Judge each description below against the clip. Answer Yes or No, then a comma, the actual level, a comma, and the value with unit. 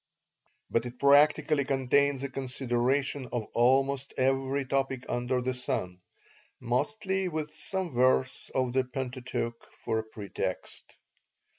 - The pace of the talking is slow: Yes, slow, 120 wpm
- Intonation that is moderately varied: No, narrow, 2.3 semitones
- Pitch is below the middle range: Yes, low, 130 Hz